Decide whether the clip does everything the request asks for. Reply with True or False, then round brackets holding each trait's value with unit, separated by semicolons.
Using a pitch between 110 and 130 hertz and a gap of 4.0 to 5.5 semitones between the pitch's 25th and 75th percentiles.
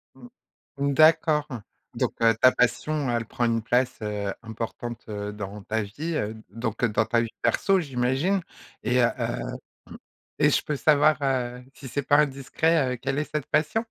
True (125 Hz; 4.7 semitones)